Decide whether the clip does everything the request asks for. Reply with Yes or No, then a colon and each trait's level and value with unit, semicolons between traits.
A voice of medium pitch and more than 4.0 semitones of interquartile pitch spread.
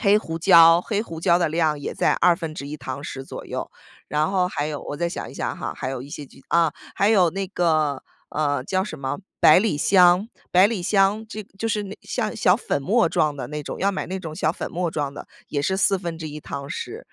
Yes: medium, 170 Hz; average, 4.5 semitones